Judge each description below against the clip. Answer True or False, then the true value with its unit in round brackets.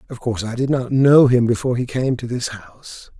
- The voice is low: True (125 Hz)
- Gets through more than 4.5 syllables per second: True (5.8 syllables/s)